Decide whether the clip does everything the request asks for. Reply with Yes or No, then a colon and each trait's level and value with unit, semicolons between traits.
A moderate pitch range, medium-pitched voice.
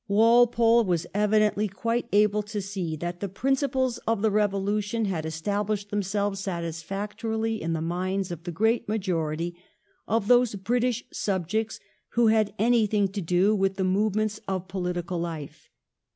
No: average, 3.1 semitones; high, 205 Hz